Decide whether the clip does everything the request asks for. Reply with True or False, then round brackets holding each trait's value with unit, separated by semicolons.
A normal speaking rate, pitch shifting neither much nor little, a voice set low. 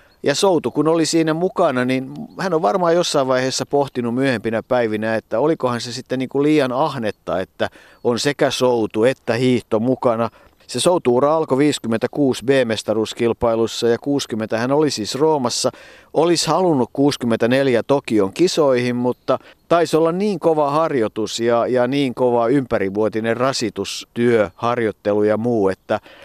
True (140 wpm; 4.0 semitones; 125 Hz)